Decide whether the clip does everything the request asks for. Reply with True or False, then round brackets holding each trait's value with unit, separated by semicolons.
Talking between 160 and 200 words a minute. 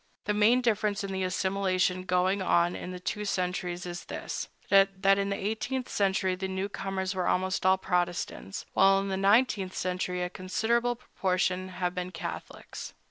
True (165 wpm)